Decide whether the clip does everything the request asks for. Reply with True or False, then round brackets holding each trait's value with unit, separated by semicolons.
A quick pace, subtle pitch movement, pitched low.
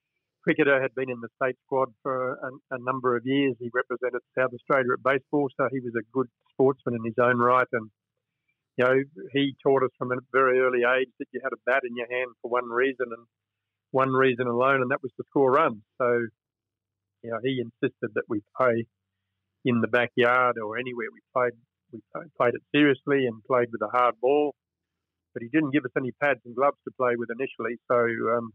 True (210 wpm; 2.1 semitones; 125 Hz)